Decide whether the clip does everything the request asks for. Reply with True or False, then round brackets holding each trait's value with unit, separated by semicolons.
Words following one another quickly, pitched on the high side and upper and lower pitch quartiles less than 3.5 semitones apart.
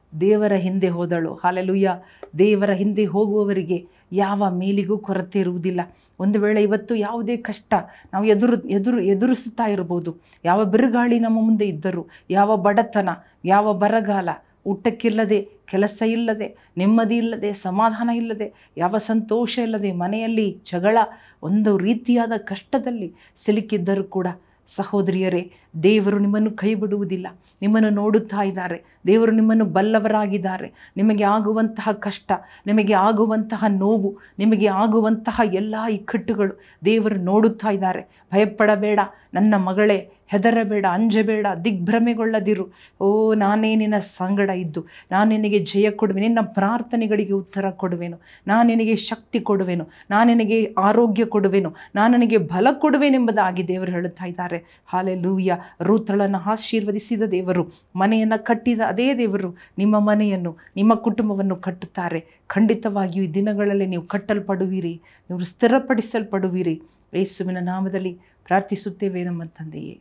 True (110 wpm; 205 Hz; 2.6 semitones)